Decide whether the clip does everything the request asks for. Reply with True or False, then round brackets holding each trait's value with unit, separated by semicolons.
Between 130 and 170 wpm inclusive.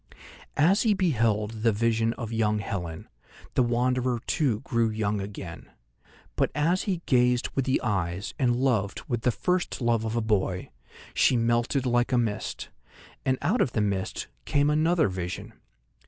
True (160 wpm)